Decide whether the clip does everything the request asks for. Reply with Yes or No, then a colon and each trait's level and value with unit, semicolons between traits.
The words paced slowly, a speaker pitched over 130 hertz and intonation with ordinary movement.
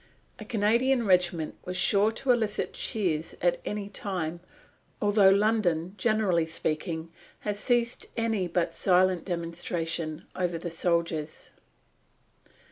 Yes: slow, 115 wpm; medium, 185 Hz; average, 4.0 semitones